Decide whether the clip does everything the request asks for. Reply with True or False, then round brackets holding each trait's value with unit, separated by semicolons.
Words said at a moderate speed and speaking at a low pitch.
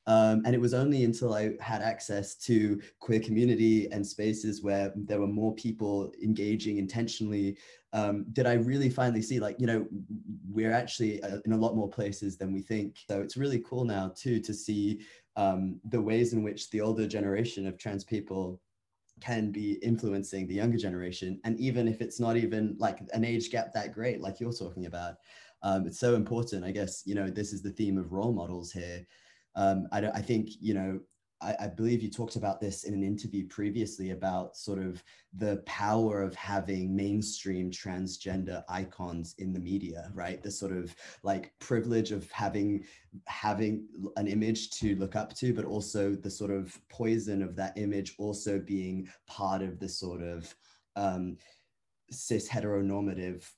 True (180 wpm; 105 Hz)